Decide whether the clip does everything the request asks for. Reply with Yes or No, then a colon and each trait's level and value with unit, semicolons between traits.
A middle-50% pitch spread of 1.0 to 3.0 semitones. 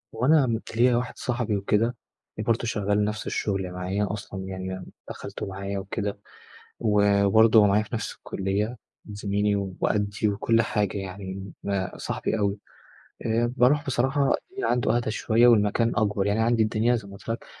Yes: average, 2.7 semitones